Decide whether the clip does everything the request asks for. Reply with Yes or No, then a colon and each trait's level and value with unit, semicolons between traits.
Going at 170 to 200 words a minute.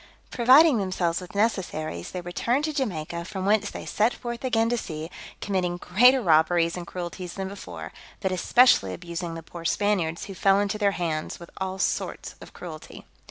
Yes: average, 175 wpm